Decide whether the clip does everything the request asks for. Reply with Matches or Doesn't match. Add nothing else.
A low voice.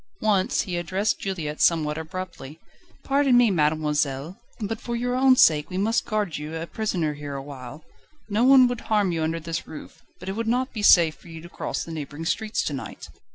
Doesn't match